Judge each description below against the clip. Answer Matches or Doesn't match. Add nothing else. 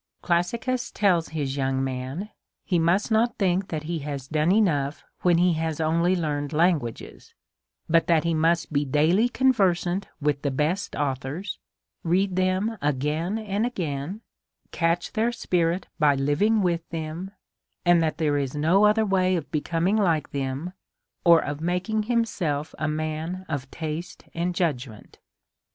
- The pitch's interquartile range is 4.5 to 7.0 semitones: Doesn't match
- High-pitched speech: Doesn't match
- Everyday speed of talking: Matches